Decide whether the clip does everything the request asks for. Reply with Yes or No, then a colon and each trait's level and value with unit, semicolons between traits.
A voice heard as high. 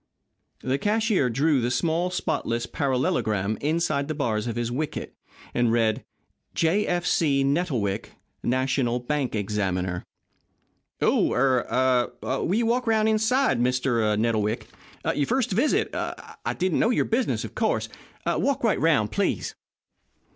No: low, 135 Hz